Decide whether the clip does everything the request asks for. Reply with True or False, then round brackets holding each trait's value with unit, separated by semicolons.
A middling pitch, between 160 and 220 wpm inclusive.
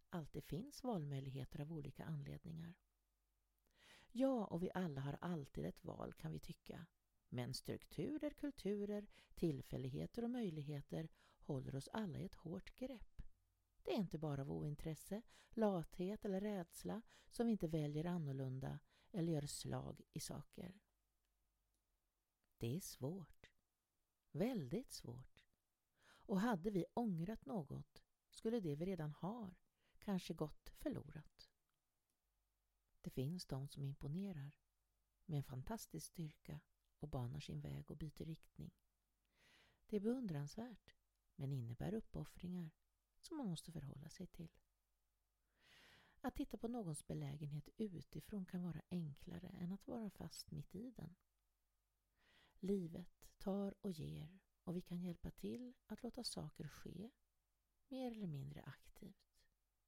False (170 Hz; 130 wpm)